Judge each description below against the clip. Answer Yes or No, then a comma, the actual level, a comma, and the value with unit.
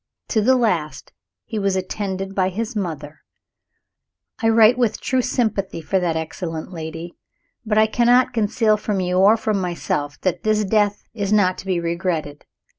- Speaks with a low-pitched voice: No, high, 195 Hz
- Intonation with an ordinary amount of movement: Yes, average, 3.8 semitones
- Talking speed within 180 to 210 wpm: No, average, 165 wpm